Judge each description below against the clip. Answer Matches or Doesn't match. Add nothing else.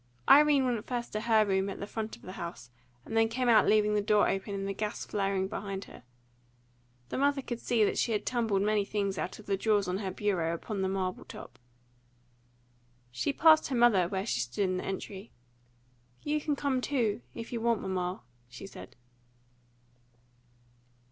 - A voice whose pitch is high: Matches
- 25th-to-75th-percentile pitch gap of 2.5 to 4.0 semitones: Matches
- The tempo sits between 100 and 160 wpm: Doesn't match